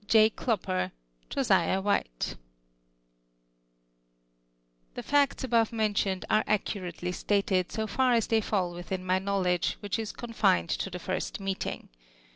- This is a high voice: Yes, high, 200 Hz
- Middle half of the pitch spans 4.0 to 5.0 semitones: No, average, 3.2 semitones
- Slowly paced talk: Yes, slow, 125 wpm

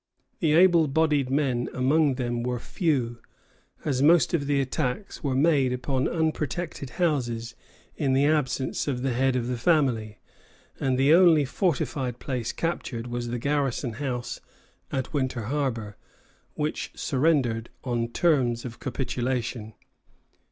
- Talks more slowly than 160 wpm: Yes, slow, 135 wpm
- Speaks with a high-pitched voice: No, low, 130 Hz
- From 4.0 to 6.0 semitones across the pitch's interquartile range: No, average, 3.6 semitones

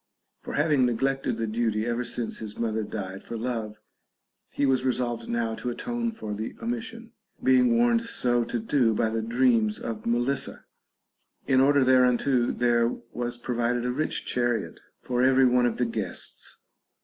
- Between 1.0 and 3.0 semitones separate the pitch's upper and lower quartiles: Yes, average, 2.7 semitones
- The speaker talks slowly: No, average, 160 wpm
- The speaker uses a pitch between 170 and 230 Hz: No, low, 120 Hz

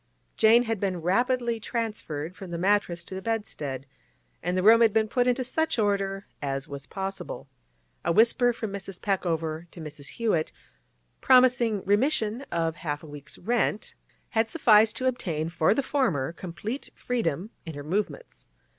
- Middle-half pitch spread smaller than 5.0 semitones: No, wide, 5.6 semitones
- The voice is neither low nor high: No, high, 200 Hz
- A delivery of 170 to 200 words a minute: No, average, 160 wpm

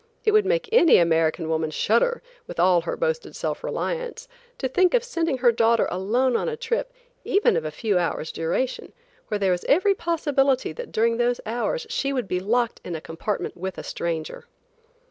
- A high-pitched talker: Yes, high, 245 Hz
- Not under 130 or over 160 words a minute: No, average, 190 wpm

